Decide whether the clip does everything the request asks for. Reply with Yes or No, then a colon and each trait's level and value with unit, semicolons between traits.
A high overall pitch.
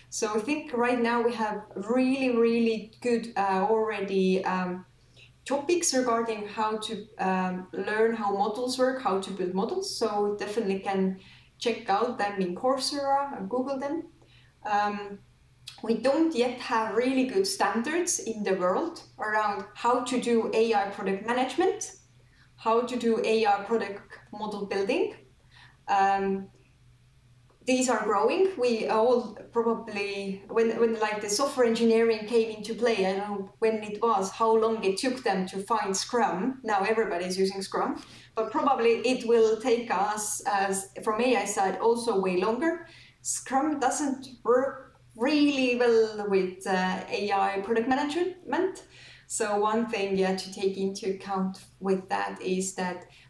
Yes: high, 220 Hz